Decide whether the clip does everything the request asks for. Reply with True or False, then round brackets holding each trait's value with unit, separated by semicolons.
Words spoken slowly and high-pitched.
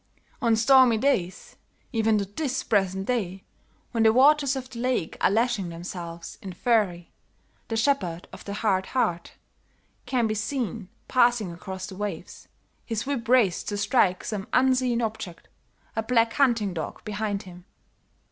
False (150 wpm; 220 Hz)